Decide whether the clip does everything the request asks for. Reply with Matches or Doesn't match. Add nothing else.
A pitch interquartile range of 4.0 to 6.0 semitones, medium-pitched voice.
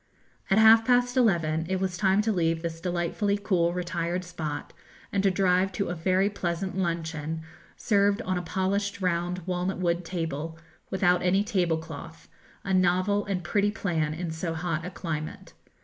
Doesn't match